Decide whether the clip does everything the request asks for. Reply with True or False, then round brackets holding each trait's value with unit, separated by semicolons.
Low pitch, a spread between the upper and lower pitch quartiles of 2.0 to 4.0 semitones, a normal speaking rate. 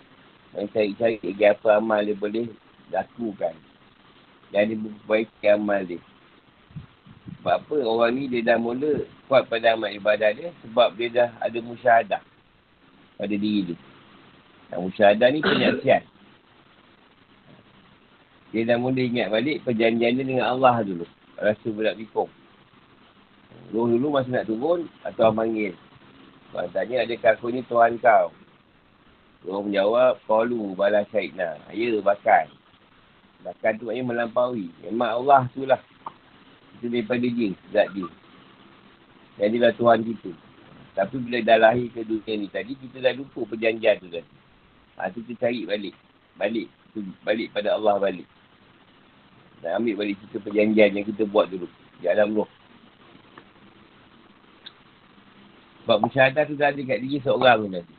True (110 Hz; 2.8 semitones; 140 wpm)